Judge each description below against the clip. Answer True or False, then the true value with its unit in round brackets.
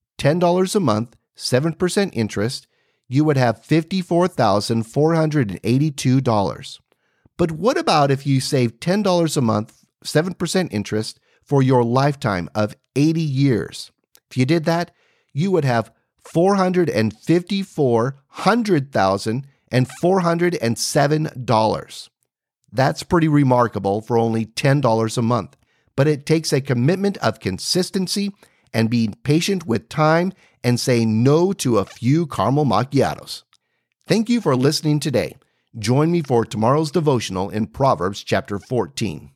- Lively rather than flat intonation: True (6.6 semitones)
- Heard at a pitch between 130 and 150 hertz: True (140 Hz)